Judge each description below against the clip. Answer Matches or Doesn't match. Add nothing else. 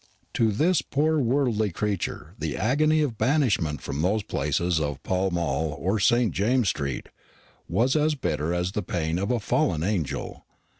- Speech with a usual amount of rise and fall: Doesn't match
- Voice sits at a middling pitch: Doesn't match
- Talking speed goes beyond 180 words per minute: Doesn't match